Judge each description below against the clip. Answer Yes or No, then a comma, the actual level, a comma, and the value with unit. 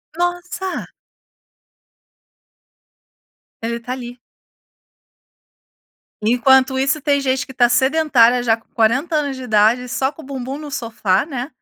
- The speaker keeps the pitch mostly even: No, average, 3.1 semitones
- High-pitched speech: Yes, very high, 260 Hz